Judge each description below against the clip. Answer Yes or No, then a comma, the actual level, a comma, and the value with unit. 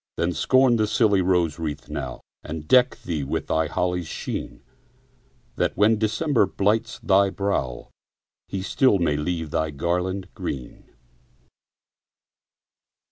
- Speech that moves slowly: Yes, slow, 125 wpm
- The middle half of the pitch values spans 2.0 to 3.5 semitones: No, average, 4.7 semitones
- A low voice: Yes, very low, 90 Hz